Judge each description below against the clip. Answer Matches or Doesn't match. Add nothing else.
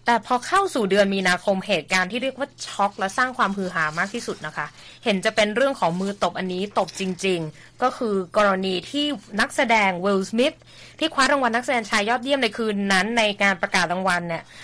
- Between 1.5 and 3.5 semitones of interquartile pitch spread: Doesn't match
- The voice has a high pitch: Matches